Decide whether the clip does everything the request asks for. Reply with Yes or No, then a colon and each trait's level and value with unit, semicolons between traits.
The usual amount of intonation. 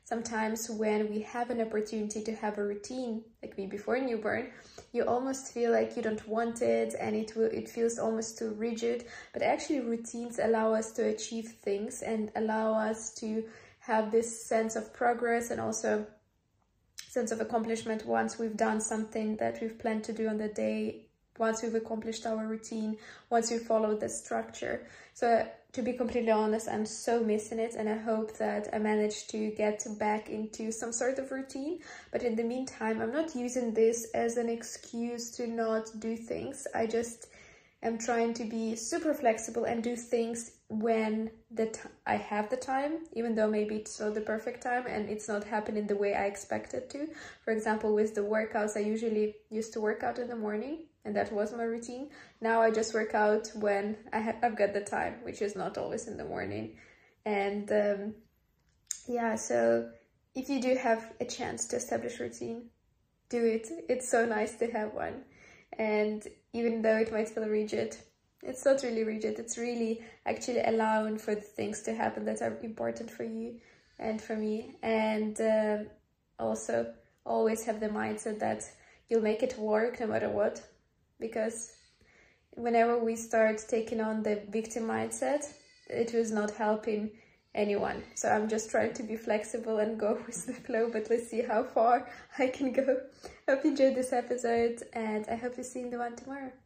No: narrow, 1.5 semitones